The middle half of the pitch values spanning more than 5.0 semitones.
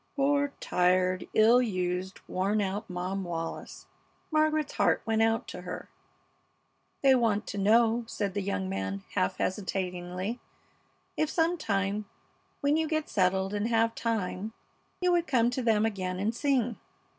No: average, 4.7 semitones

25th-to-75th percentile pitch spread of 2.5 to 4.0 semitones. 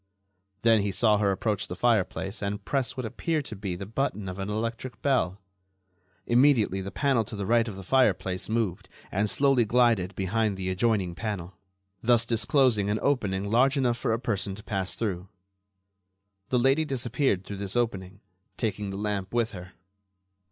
Yes: average, 3.7 semitones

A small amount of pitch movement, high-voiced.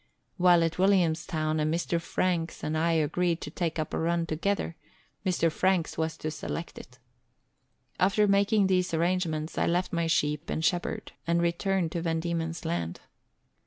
No: narrow, 2.2 semitones; medium, 170 Hz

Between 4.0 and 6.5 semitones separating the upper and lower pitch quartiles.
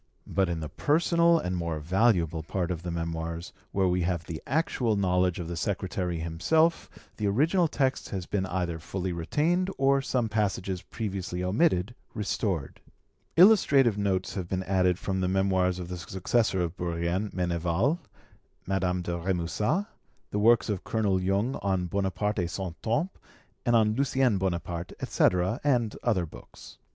Yes: average, 4.3 semitones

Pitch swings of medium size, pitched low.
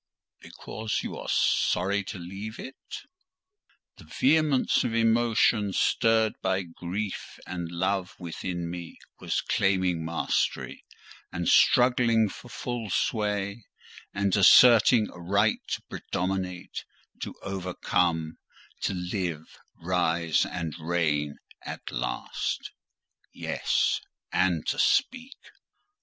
Yes: average, 4.1 semitones; very low, 95 Hz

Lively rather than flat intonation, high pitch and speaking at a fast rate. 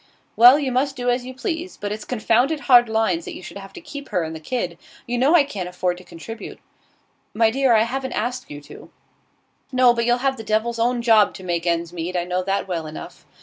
Yes: wide, 5.9 semitones; high, 230 Hz; fast, 235 wpm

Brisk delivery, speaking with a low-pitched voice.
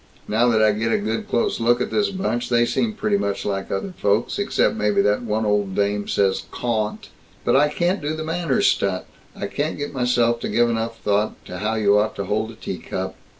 Yes: fast, 225 wpm; low, 115 Hz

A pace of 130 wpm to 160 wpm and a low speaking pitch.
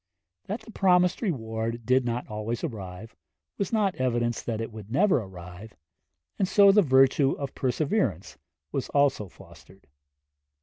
Yes: slow, 135 wpm; low, 125 Hz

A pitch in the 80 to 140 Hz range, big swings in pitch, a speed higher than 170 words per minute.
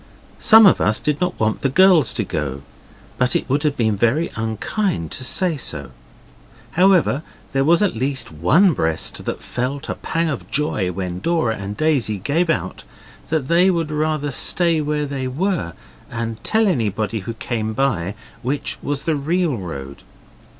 No: low, 135 Hz; wide, 7.1 semitones; average, 165 wpm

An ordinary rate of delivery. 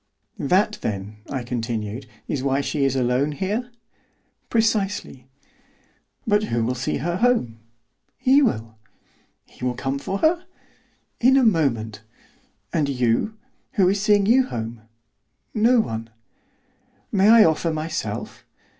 No: slow, 130 wpm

